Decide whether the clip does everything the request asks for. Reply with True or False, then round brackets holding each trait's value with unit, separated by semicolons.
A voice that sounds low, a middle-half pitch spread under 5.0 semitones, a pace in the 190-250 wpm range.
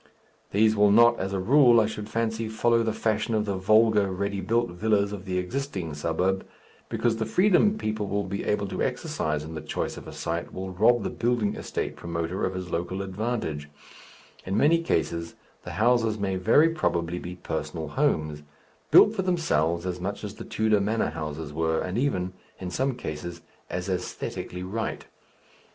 False (100 Hz; 4.2 semitones; 180 wpm)